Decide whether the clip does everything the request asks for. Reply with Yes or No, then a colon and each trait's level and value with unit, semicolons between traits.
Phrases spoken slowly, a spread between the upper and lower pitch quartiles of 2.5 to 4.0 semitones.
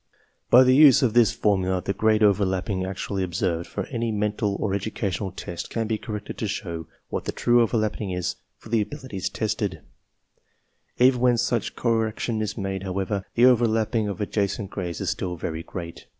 No: average, 175 wpm; average, 3.1 semitones